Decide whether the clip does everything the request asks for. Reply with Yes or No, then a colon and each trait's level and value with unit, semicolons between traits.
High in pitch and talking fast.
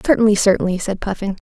No: high, 200 Hz; average, 160 wpm